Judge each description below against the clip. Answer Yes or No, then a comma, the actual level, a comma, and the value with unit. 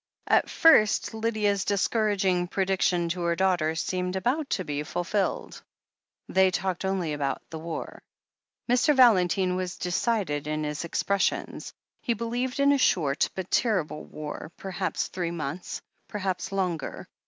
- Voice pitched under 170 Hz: No, medium, 185 Hz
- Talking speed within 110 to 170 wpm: Yes, average, 140 wpm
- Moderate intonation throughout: Yes, average, 3.8 semitones